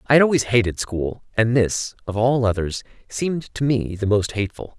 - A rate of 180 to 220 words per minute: Yes, average, 200 wpm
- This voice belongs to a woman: No, male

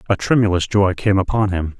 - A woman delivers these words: No, male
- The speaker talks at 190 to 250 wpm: Yes, average, 200 wpm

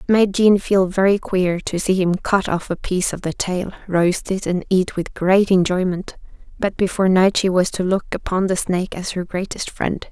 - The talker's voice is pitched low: No, medium, 185 Hz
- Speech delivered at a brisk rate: Yes, fast, 220 wpm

